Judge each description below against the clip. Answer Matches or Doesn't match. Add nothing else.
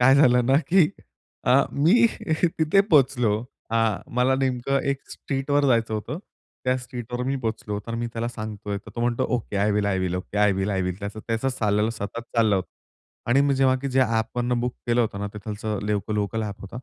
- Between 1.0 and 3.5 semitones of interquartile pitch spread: Doesn't match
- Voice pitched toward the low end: Matches